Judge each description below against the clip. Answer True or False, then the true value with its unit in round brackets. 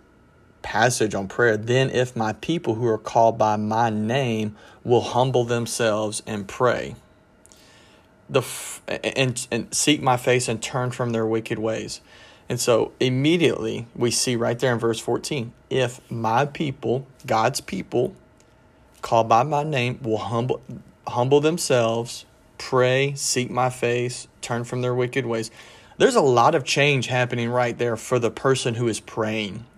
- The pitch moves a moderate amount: False (2.1 semitones)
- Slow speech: False (155 wpm)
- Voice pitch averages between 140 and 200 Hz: False (120 Hz)